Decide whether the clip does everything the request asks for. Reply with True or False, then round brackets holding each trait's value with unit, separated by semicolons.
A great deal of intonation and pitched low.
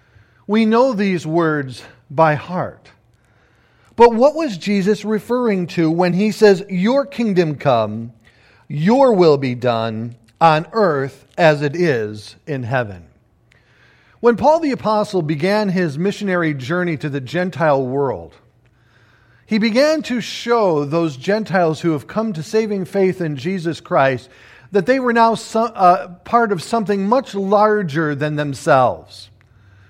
False (8.3 semitones; 170 Hz)